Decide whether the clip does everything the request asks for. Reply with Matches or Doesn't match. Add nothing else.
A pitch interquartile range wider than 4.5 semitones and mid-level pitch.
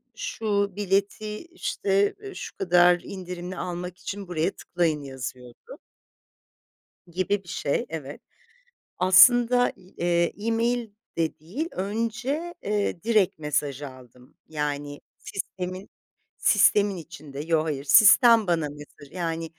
Matches